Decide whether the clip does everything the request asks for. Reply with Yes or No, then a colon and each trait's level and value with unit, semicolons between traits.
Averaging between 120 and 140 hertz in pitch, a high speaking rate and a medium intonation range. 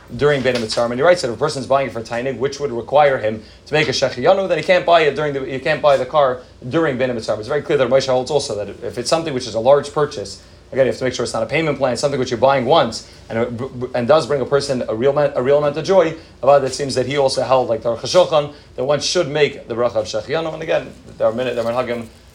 Yes: low, 135 Hz; fast, 295 wpm; average, 3.4 semitones